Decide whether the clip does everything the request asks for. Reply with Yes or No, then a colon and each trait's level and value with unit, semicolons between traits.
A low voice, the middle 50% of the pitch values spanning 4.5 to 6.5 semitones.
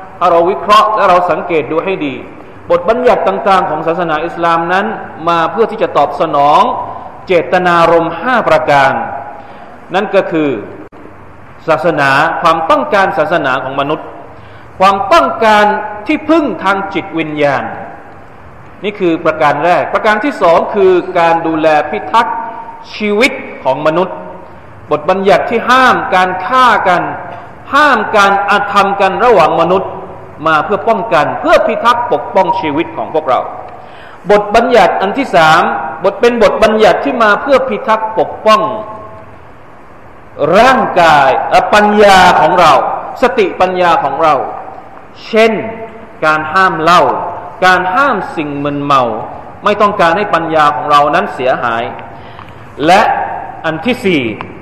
No: high, 190 Hz; average, 5.2 semitones